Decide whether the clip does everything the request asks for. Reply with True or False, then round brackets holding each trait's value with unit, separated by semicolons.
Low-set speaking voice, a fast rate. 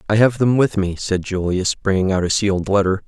True (100 Hz; 235 wpm)